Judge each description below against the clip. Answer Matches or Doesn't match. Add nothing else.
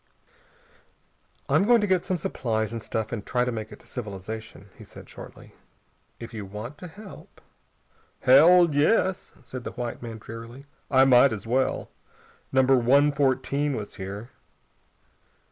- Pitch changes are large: Doesn't match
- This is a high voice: Doesn't match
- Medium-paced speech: Matches